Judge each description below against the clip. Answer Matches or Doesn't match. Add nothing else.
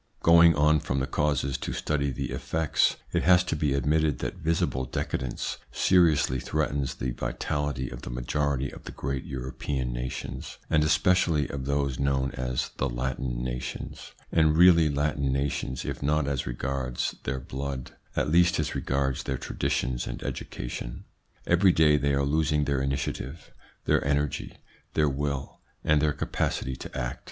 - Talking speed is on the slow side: Doesn't match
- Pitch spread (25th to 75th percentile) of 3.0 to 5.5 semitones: Doesn't match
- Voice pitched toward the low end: Matches